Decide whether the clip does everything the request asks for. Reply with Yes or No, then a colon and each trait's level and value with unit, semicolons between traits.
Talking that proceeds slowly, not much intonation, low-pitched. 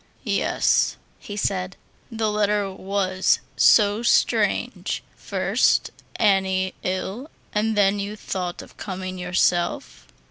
No: slow, 105 wpm; narrow, 2.0 semitones; high, 195 Hz